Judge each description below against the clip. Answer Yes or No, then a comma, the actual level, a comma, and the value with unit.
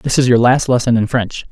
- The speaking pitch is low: Yes, low, 120 Hz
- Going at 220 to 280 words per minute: Yes, fast, 275 wpm